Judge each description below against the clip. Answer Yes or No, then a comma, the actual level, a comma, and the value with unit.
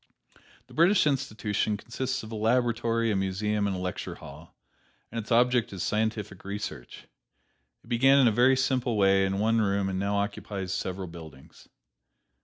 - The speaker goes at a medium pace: Yes, average, 165 wpm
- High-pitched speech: No, low, 105 Hz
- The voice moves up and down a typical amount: Yes, average, 3.6 semitones